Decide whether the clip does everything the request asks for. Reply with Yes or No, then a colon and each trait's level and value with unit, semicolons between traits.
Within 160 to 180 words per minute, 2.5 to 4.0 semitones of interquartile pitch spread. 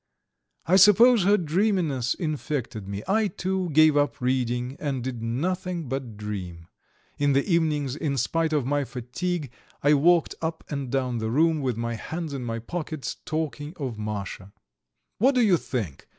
No: average, 165 wpm; wide, 5.4 semitones